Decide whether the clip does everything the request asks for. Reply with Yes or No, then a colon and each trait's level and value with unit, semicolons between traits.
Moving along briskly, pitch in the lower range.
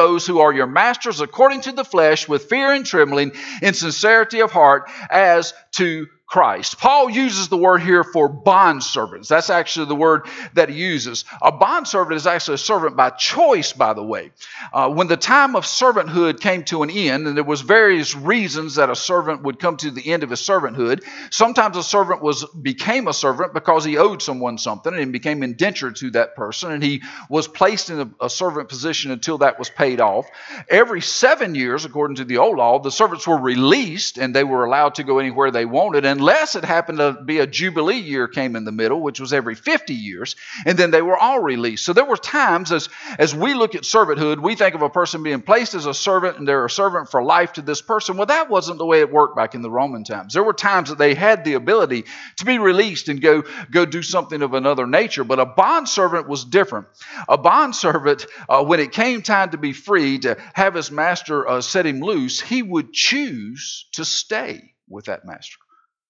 No: fast, 220 wpm; medium, 165 Hz